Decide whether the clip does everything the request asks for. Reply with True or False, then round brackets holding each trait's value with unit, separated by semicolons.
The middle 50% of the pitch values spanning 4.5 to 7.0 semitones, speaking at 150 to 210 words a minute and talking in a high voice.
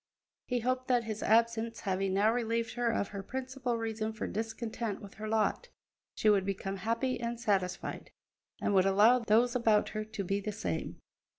False (2.6 semitones; 180 wpm; 220 Hz)